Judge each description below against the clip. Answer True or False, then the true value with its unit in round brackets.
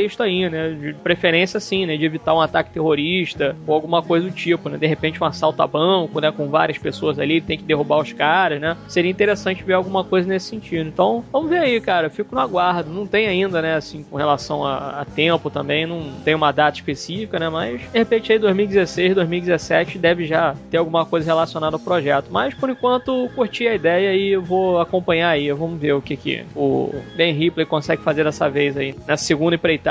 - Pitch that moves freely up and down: False (3.2 semitones)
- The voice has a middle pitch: True (165 Hz)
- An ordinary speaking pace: False (220 wpm)